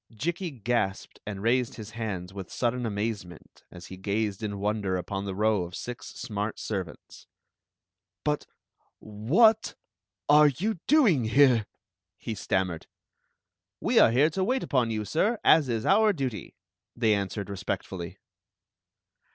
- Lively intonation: Yes, wide, 5.8 semitones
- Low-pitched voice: Yes, low, 110 Hz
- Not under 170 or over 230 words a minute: No, average, 145 wpm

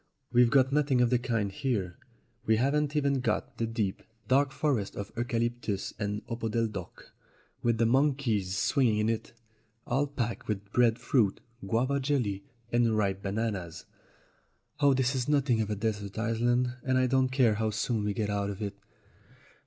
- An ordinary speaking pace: Yes, average, 165 wpm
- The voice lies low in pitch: Yes, low, 115 Hz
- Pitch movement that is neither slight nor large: Yes, average, 3.8 semitones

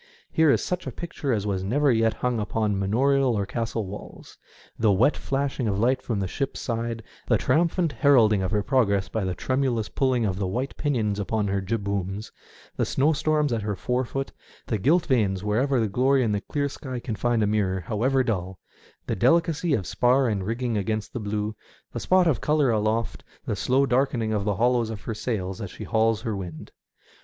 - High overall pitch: No, low, 115 Hz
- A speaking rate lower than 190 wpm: No, average, 200 wpm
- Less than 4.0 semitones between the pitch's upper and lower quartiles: No, average, 4.5 semitones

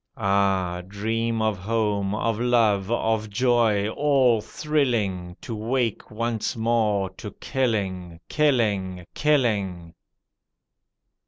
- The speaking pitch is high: No, low, 110 Hz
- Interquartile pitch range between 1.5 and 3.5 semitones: Yes, average, 3.2 semitones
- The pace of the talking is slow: Yes, slow, 95 wpm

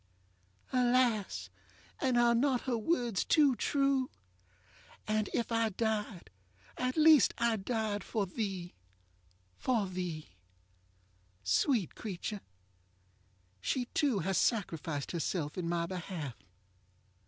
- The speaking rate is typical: No, slow, 105 wpm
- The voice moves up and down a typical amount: No, wide, 6.2 semitones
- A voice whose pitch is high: Yes, high, 210 Hz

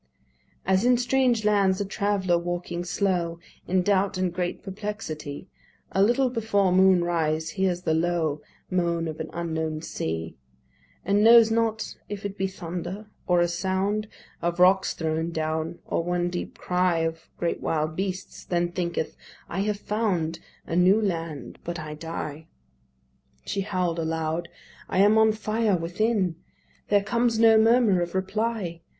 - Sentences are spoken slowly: No, average, 150 wpm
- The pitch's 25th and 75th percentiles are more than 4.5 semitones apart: No, average, 3.6 semitones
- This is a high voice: No, medium, 180 Hz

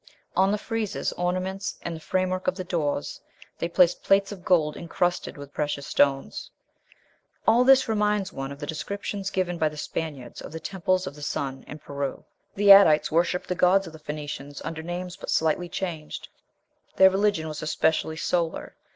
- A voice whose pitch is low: No, medium, 175 Hz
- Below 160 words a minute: No, average, 175 wpm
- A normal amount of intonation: Yes, average, 3.8 semitones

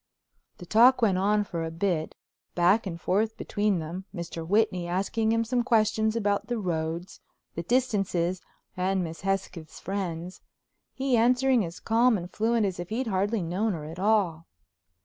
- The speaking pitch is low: No, high, 195 Hz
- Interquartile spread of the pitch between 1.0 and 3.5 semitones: No, average, 4.4 semitones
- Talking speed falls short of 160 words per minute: No, average, 165 wpm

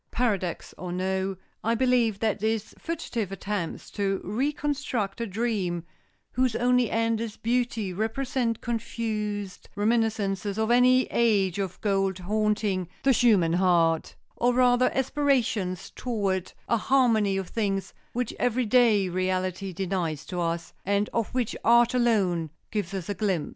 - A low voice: No, high, 210 Hz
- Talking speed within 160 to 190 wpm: No, average, 140 wpm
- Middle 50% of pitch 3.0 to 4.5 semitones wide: Yes, average, 3.8 semitones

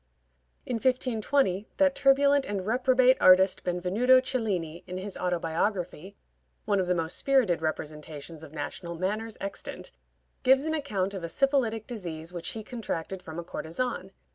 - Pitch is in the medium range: No, high, 195 Hz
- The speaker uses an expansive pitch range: Yes, wide, 6.6 semitones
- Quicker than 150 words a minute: No, average, 145 wpm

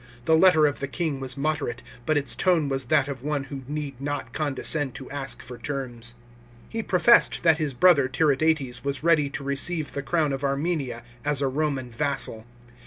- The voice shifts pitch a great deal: No, narrow, 2.5 semitones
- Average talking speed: Yes, average, 190 wpm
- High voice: No, medium, 140 Hz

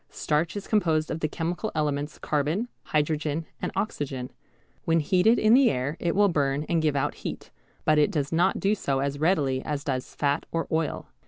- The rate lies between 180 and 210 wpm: Yes, average, 190 wpm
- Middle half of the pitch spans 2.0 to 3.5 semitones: Yes, average, 3.2 semitones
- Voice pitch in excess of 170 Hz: No, medium, 155 Hz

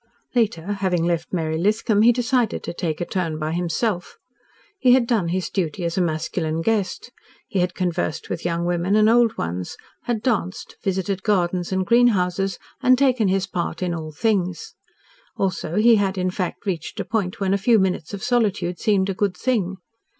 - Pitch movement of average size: Yes, average, 3.8 semitones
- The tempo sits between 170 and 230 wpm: Yes, average, 185 wpm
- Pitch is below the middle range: No, high, 190 Hz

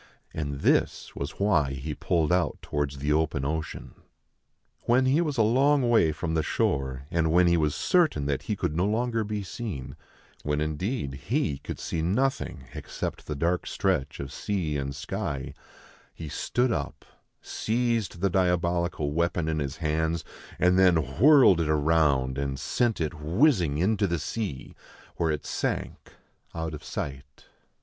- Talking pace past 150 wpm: Yes, average, 160 wpm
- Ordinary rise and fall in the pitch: No, wide, 5.9 semitones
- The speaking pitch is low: Yes, very low, 80 Hz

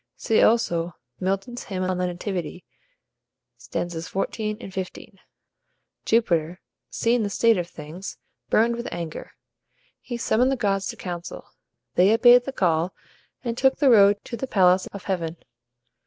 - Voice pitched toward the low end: No, high, 195 Hz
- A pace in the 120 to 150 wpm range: Yes, average, 145 wpm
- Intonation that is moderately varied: Yes, average, 4.7 semitones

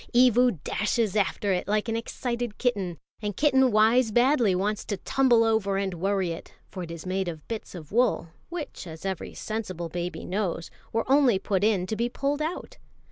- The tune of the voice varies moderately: Yes, average, 4.5 semitones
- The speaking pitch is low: No, high, 210 Hz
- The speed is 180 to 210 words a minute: Yes, average, 190 wpm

